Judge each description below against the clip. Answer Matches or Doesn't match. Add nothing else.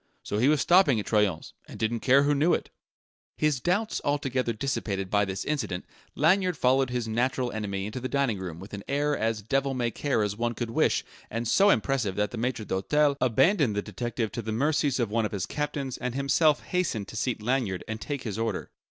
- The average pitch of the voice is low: Matches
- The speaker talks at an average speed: Doesn't match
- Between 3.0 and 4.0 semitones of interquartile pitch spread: Doesn't match